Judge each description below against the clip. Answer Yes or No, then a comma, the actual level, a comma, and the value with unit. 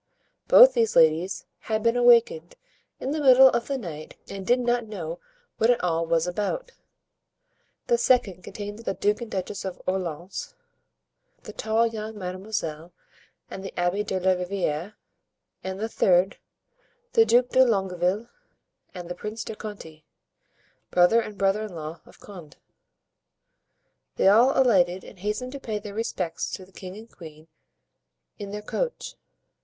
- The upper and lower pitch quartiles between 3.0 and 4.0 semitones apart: No, average, 4.5 semitones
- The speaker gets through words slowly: No, average, 155 wpm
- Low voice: No, high, 200 Hz